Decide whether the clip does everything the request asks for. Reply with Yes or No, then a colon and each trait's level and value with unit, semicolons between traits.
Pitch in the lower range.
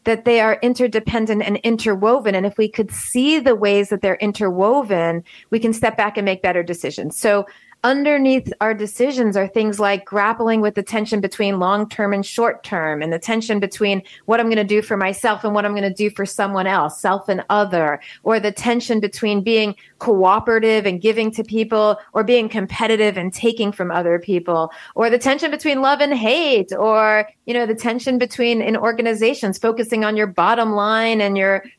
No: high, 215 Hz